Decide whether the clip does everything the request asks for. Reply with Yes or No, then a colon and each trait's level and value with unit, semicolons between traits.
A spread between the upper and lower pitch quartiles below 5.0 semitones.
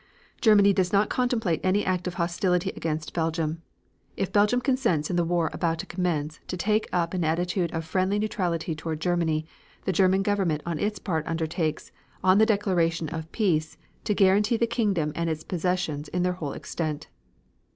Yes: average, 3.5 semitones